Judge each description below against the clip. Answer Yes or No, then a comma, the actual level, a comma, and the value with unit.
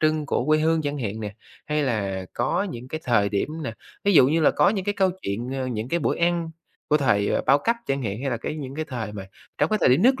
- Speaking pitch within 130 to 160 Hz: Yes, medium, 140 Hz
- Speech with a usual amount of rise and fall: No, wide, 5.7 semitones